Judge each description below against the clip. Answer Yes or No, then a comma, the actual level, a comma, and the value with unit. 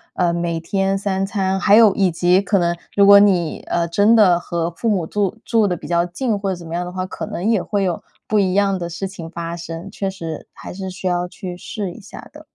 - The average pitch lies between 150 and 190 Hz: Yes, medium, 185 Hz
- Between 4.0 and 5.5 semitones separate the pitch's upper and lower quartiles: No, average, 2.7 semitones